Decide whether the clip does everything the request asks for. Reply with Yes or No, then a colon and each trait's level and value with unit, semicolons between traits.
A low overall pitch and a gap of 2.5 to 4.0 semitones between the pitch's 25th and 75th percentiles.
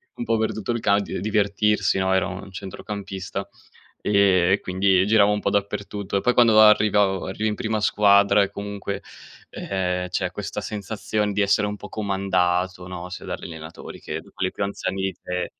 No: low, 100 Hz; narrow, 1.8 semitones